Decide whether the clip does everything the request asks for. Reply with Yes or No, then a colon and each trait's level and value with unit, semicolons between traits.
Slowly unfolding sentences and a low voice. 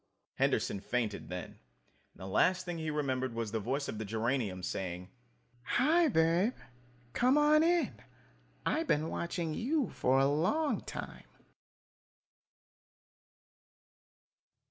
No: slow, 120 wpm; medium, 150 Hz